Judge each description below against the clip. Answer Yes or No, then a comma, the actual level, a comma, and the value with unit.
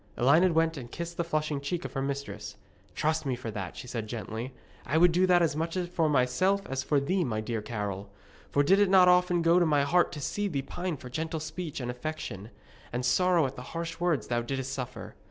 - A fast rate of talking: Yes, fast, 225 wpm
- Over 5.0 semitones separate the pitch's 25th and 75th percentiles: Yes, wide, 5.5 semitones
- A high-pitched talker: No, medium, 150 Hz